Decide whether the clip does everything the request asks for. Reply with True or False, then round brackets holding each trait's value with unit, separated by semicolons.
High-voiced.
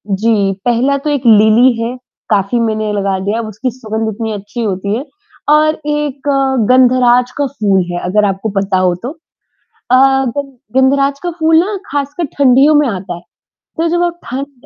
True (245 Hz)